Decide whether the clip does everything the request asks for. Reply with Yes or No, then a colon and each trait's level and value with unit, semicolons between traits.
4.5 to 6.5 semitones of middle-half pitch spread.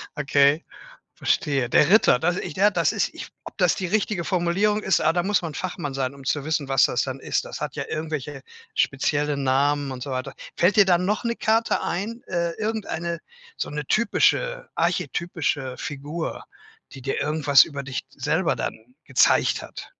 Yes: average, 5.2 semitones